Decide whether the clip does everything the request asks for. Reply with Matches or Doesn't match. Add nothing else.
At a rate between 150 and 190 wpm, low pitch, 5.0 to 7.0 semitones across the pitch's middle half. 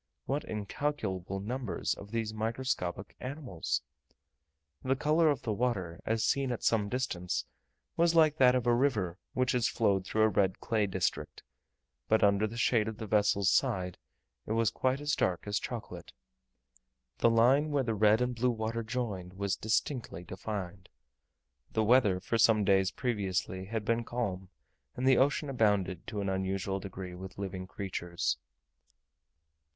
Doesn't match